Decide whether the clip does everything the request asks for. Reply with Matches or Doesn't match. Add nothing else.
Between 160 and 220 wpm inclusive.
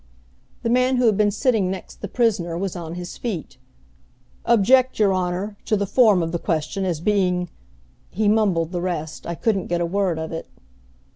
Matches